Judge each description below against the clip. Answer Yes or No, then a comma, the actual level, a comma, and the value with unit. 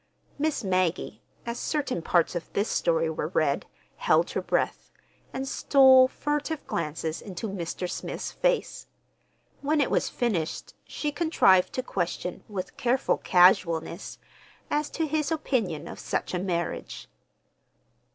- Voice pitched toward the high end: Yes, high, 200 Hz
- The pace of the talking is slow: Yes, slow, 130 wpm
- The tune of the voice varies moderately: No, wide, 8.4 semitones